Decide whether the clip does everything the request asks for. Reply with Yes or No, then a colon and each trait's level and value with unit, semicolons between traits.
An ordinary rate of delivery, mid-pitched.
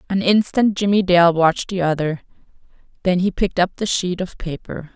Yes: average, 180 wpm; medium, 180 Hz